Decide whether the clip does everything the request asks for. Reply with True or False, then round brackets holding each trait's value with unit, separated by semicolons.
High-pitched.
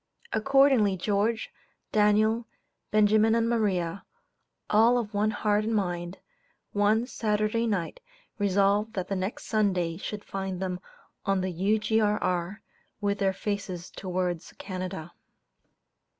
True (205 Hz)